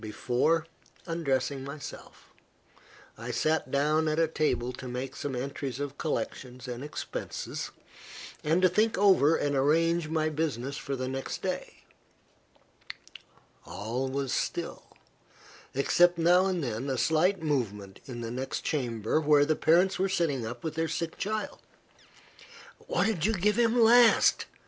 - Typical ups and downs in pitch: Yes, average, 4.4 semitones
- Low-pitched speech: No, medium, 150 Hz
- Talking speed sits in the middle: Yes, average, 145 wpm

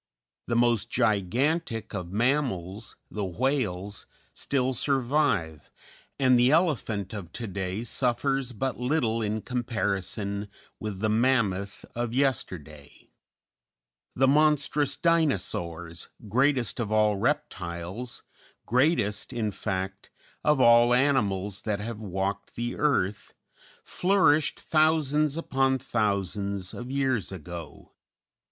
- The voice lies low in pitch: Yes, low, 115 Hz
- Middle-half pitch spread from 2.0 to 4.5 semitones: No, average, 5.2 semitones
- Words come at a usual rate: No, slow, 105 wpm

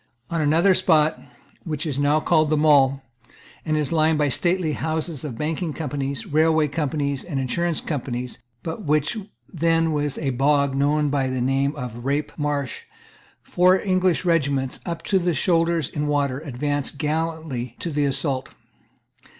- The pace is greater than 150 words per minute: Yes, average, 160 wpm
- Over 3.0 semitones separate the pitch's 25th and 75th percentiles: No, average, 2.7 semitones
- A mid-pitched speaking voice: Yes, medium, 150 Hz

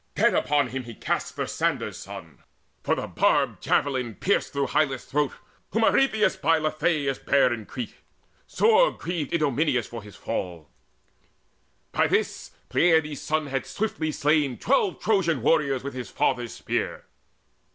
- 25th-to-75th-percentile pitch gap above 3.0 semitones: Yes, average, 4.3 semitones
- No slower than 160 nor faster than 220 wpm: No, average, 140 wpm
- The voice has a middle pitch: Yes, medium, 145 Hz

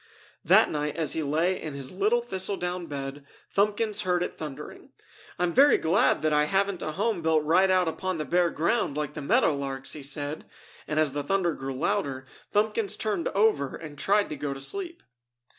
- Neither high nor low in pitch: Yes, medium, 165 Hz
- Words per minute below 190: No, average, 195 wpm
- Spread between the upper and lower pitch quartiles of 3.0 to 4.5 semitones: No, average, 5.2 semitones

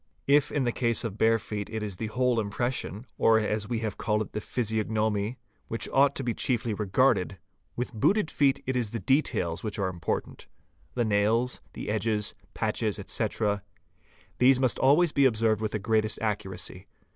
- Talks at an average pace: Yes, average, 190 wpm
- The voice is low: Yes, low, 110 Hz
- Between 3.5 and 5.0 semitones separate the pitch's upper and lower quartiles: No, average, 3.1 semitones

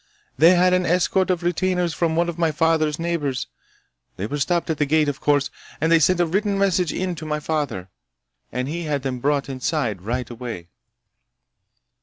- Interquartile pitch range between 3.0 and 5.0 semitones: Yes, average, 3.8 semitones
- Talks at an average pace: Yes, average, 190 wpm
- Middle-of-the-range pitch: Yes, medium, 155 Hz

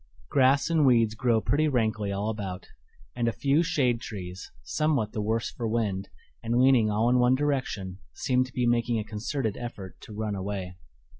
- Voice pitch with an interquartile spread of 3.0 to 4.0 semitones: Yes, average, 3.5 semitones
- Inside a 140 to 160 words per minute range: No, average, 180 wpm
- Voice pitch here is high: No, low, 115 Hz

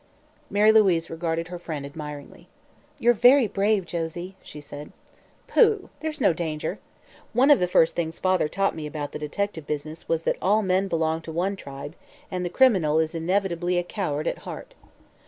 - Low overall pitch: No, medium, 175 Hz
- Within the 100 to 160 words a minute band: No, average, 175 wpm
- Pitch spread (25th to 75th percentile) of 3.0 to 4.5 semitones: Yes, average, 3.9 semitones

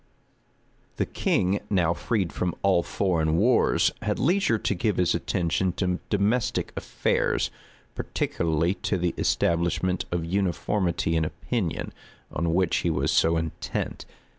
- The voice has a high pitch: No, very low, 90 Hz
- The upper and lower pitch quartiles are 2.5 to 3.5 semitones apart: Yes, average, 3.0 semitones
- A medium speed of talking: No, slow, 130 wpm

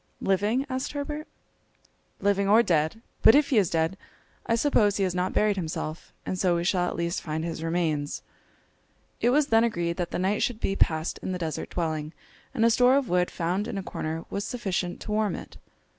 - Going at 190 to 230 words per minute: Yes, fast, 205 wpm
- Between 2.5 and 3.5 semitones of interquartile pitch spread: No, average, 4.8 semitones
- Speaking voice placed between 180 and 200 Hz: Yes, high, 190 Hz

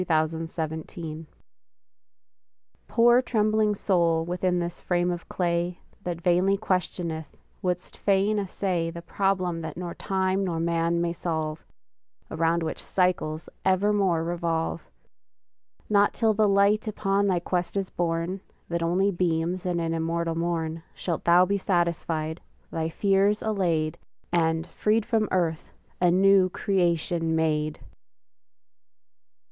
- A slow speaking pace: Yes, slow, 125 wpm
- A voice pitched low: No, medium, 175 Hz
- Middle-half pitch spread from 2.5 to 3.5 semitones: Yes, average, 2.9 semitones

